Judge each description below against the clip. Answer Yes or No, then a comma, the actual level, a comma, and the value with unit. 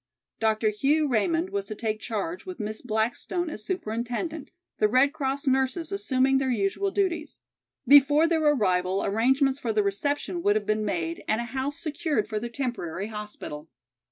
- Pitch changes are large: Yes, wide, 5.9 semitones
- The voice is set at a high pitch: Yes, very high, 255 Hz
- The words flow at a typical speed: Yes, average, 165 wpm